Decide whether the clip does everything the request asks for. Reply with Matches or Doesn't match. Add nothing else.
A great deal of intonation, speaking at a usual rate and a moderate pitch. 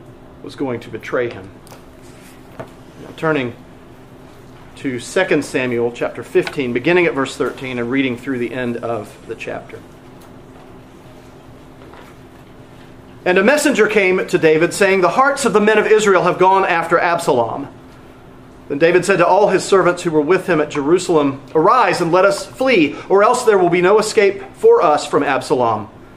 Matches